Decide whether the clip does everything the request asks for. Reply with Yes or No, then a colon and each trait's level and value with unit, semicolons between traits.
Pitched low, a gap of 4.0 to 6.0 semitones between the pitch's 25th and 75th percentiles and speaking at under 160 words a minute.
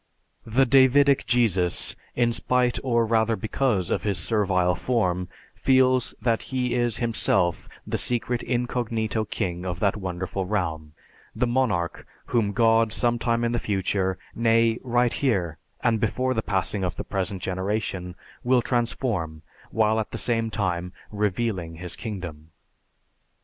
Yes: low, 110 Hz; average, 4.5 semitones; average, 140 wpm